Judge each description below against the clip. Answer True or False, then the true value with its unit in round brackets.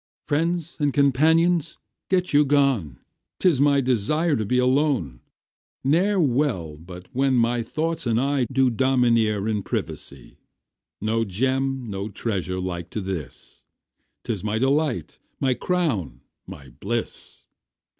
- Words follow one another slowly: True (125 wpm)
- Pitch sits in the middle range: False (125 Hz)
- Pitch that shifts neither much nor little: False (6.2 semitones)